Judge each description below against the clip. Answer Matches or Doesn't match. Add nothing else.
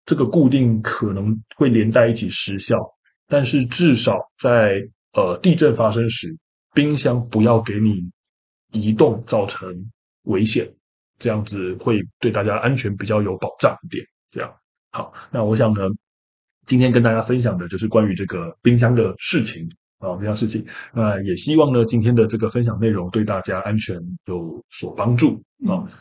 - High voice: Doesn't match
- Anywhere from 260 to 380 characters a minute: Doesn't match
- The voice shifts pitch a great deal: Doesn't match